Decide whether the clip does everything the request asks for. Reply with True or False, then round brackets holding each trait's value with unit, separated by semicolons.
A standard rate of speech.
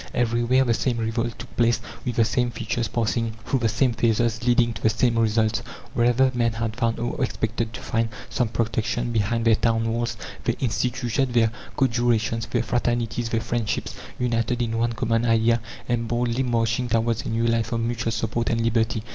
True (190 wpm)